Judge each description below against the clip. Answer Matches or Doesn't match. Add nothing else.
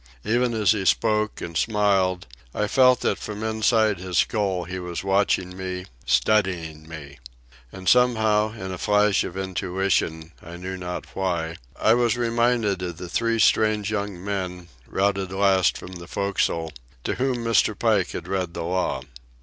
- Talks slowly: Doesn't match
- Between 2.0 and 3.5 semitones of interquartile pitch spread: Matches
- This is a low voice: Matches